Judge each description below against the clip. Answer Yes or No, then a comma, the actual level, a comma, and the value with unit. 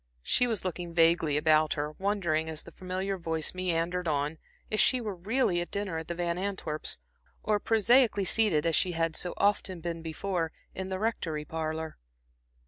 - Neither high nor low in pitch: Yes, medium, 175 Hz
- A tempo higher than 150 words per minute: Yes, average, 175 wpm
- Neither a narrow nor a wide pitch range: Yes, average, 3.6 semitones